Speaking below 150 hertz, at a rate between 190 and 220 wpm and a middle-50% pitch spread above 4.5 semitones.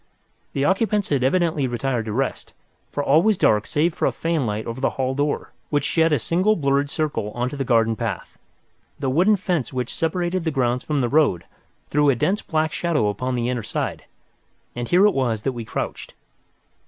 Yes: medium, 140 Hz; average, 200 wpm; average, 5.2 semitones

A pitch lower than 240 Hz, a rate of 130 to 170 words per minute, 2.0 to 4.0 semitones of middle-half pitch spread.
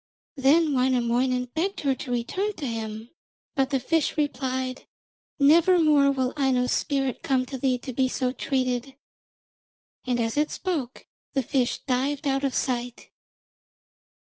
No: very high, 265 Hz; average, 140 wpm; narrow, 2.4 semitones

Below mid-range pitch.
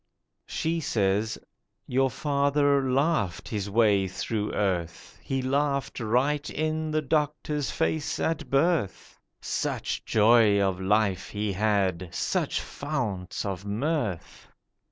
Yes: low, 115 Hz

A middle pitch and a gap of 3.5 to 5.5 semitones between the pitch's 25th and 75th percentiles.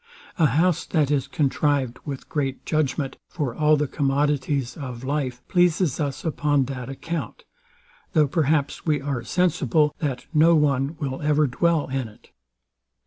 No: medium, 145 Hz; narrow, 2.4 semitones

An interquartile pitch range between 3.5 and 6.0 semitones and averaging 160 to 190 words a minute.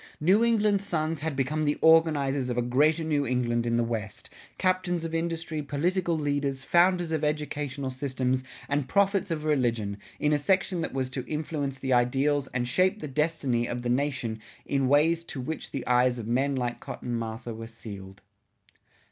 Yes: average, 4.5 semitones; average, 180 wpm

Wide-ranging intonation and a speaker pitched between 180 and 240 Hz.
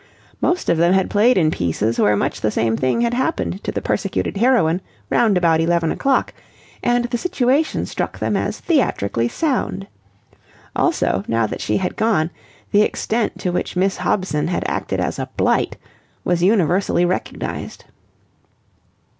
Yes: wide, 6.9 semitones; medium, 185 Hz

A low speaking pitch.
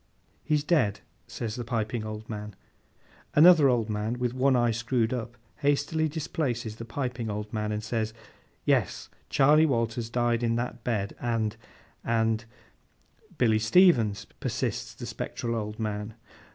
Yes: low, 115 Hz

